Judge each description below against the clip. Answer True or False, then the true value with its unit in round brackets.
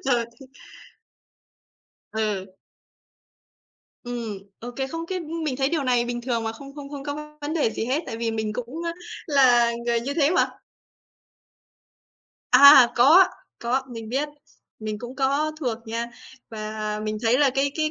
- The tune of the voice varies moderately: True (3.9 semitones)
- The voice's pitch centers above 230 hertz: True (250 Hz)